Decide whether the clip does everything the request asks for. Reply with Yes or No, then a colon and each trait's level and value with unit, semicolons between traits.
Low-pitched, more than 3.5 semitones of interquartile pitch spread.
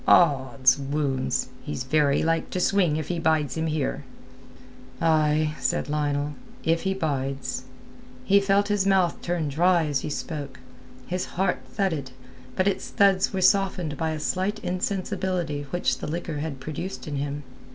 No: medium, 160 Hz; average, 4.3 semitones